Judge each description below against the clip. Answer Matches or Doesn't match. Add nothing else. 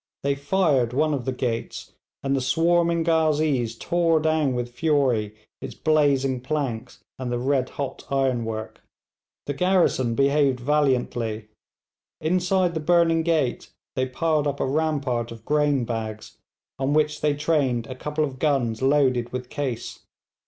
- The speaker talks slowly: Doesn't match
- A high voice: Doesn't match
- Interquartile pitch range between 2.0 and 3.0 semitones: Doesn't match